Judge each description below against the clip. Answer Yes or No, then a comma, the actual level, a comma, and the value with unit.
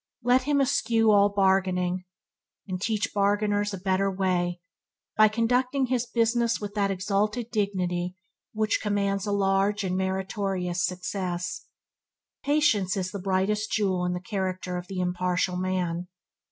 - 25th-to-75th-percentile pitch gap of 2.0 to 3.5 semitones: Yes, narrow, 2.6 semitones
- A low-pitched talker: No, high, 195 Hz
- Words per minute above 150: No, average, 140 wpm